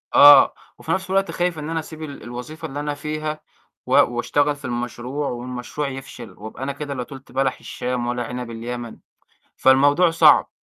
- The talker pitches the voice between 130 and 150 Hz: Yes, low, 135 Hz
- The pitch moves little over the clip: No, average, 3.7 semitones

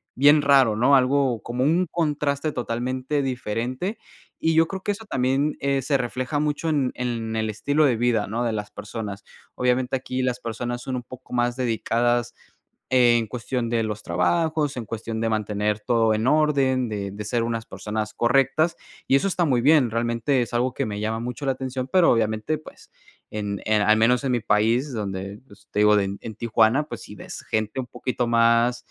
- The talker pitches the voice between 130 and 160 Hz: No, low, 120 Hz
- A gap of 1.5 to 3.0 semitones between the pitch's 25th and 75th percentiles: No, average, 3.5 semitones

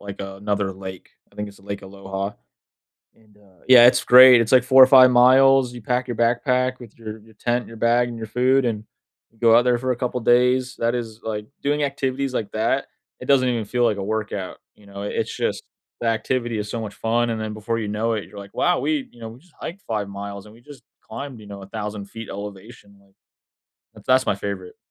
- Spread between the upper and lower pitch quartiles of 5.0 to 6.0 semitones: No, average, 3.5 semitones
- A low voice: Yes, low, 115 Hz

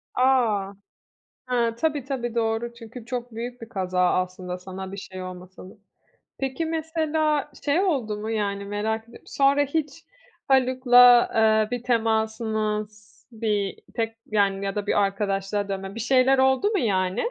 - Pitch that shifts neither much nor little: Yes, average, 4.3 semitones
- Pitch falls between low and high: No, high, 225 Hz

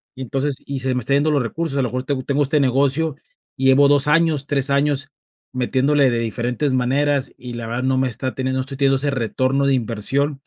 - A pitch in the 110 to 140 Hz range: Yes, low, 135 Hz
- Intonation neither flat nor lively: No, narrow, 1.8 semitones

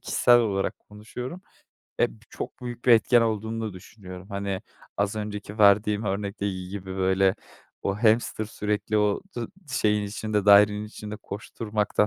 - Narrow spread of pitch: Yes, narrow, 1.6 semitones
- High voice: No, low, 105 Hz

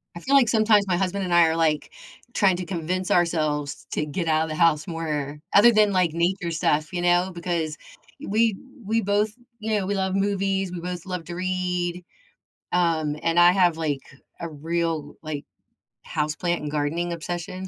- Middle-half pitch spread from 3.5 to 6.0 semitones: No, average, 2.9 semitones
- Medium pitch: Yes, medium, 175 Hz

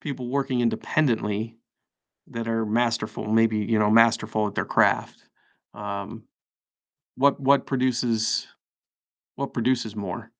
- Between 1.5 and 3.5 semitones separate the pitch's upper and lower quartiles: Yes, narrow, 2.5 semitones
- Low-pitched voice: Yes, low, 115 Hz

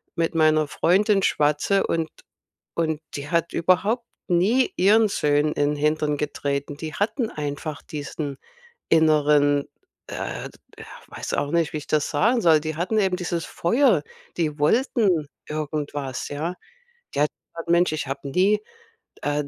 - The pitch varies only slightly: No, average, 3.8 semitones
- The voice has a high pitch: No, medium, 155 Hz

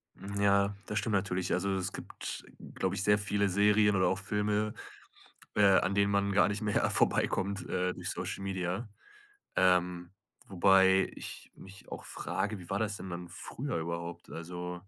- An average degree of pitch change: No, narrow, 2.0 semitones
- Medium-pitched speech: No, very low, 95 Hz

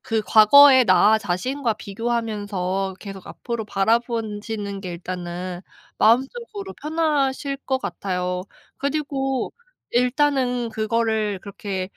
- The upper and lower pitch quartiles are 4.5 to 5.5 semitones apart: Yes, average, 5.1 semitones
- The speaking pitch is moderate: No, high, 225 Hz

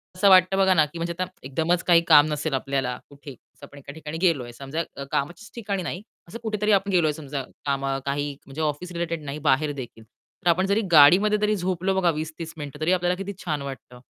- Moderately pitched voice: Yes, medium, 160 Hz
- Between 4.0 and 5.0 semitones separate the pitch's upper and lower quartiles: Yes, average, 4.5 semitones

